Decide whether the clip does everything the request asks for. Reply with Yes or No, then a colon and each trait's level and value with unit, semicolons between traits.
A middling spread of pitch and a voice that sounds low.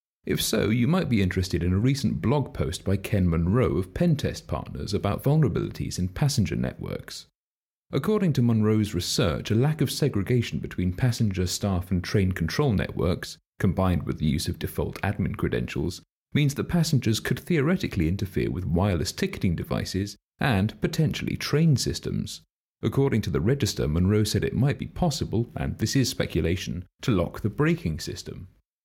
No: wide, 6.7 semitones; low, 105 Hz